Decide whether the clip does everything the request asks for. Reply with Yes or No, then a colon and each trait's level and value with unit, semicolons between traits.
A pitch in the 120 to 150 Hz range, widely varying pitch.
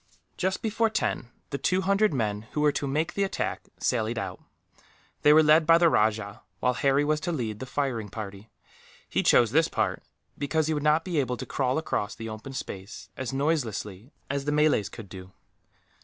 Yes: low, 135 Hz; wide, 6.1 semitones